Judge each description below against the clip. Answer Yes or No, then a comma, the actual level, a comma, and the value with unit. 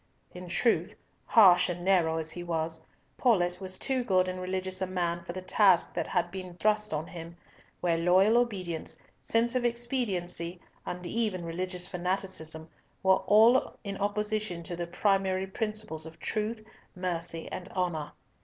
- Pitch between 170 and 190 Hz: Yes, medium, 185 Hz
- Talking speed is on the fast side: No, average, 155 wpm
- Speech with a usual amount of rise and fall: Yes, average, 3.3 semitones